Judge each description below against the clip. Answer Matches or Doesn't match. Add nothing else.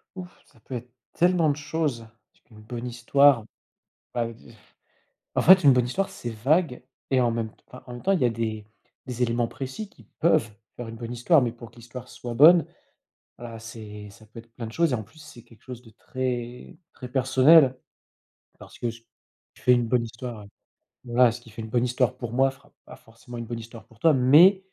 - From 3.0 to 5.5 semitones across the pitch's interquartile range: Doesn't match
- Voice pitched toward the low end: Matches